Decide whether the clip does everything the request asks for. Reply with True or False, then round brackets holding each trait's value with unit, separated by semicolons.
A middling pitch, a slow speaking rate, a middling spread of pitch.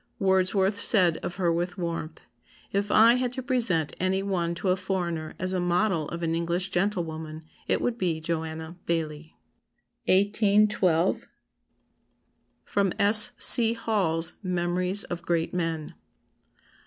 True (180 Hz; 130 wpm; 3.2 semitones)